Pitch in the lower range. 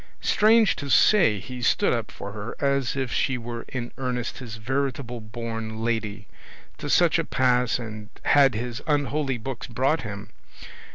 Yes: low, 125 Hz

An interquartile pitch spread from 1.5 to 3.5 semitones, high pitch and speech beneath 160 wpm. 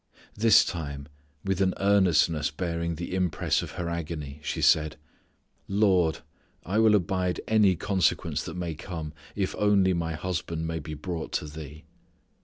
No: average, 3.2 semitones; very low, 85 Hz; average, 150 wpm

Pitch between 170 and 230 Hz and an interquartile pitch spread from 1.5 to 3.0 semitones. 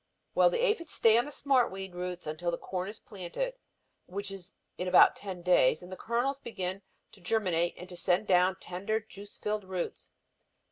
No: high, 190 Hz; average, 3.6 semitones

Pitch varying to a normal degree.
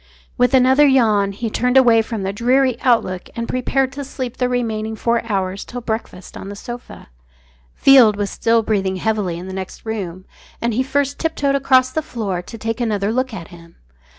Yes: average, 4.2 semitones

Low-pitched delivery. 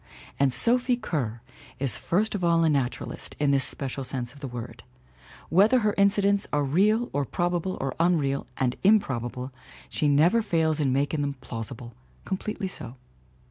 No: medium, 150 Hz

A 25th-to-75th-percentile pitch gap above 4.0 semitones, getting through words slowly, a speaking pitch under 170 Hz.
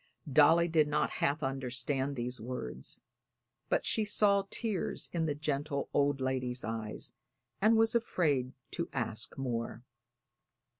Yes: average, 4.7 semitones; slow, 130 wpm; medium, 140 Hz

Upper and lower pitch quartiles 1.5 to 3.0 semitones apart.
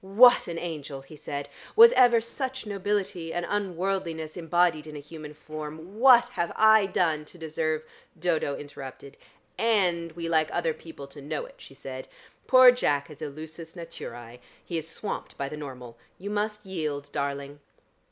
No: average, 4.9 semitones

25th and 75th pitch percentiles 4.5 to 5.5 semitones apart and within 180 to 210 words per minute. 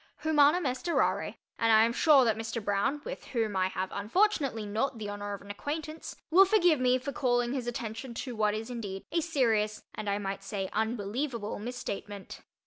Yes: average, 5.0 semitones; average, 190 wpm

